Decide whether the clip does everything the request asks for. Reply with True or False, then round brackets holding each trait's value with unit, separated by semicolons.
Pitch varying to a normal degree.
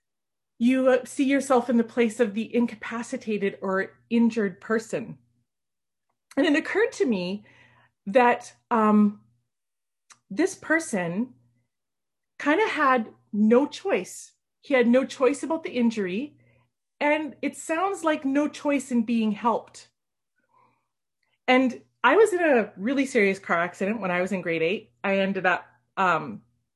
False (6.4 semitones)